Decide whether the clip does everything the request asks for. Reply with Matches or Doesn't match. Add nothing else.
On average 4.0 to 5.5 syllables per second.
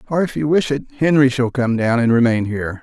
Doesn't match